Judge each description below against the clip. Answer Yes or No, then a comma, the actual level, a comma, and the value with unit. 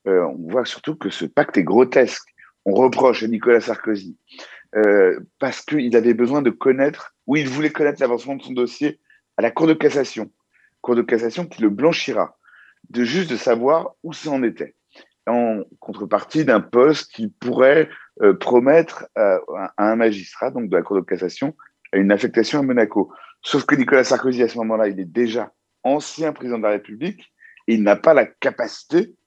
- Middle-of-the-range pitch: No, low, 120 Hz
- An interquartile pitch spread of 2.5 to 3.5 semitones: No, average, 3.9 semitones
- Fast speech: Yes, fast, 185 wpm